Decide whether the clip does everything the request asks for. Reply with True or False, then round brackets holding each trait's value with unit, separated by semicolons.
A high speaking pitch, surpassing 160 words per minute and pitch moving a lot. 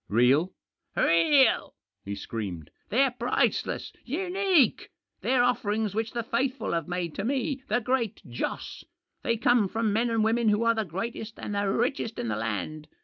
True (220 Hz; 180 wpm; 6.3 semitones)